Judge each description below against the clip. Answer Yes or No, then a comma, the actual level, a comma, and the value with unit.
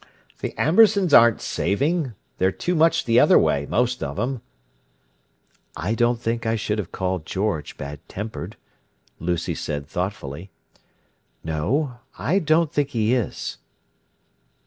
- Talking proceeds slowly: Yes, slow, 130 wpm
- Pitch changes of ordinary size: No, wide, 7.2 semitones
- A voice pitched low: Yes, low, 115 Hz